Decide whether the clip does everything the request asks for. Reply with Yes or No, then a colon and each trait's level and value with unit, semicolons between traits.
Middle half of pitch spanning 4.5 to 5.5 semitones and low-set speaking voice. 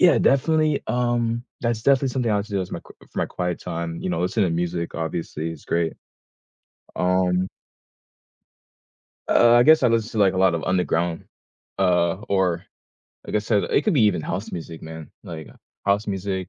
Yes: average, 5.2 semitones; very low, 95 Hz